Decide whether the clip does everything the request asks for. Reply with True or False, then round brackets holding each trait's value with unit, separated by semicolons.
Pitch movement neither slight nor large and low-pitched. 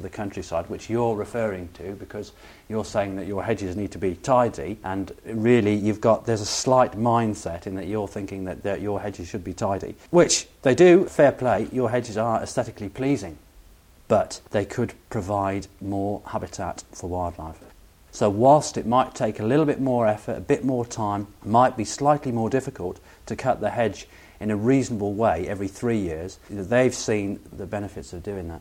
True (3.2 semitones; 105 Hz)